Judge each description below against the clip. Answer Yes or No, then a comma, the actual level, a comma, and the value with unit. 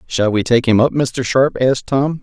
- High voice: No, low, 125 Hz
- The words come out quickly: Yes, fast, 245 wpm